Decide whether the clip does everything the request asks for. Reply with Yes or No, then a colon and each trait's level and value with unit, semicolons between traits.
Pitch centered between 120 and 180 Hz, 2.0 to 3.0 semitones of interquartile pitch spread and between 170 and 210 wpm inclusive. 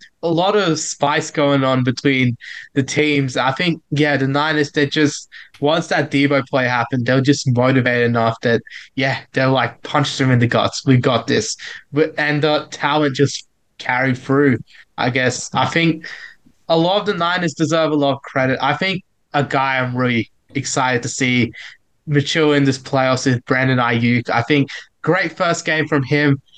Yes: medium, 140 Hz; narrow, 2.5 semitones; average, 185 wpm